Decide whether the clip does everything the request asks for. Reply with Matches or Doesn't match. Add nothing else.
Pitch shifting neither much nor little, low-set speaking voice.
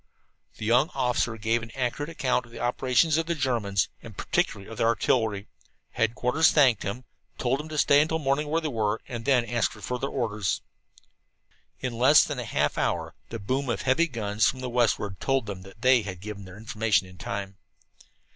Matches